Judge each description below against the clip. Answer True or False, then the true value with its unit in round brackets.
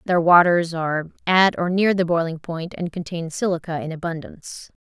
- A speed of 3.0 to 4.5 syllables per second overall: False (5.2 syllables/s)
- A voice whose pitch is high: False (170 Hz)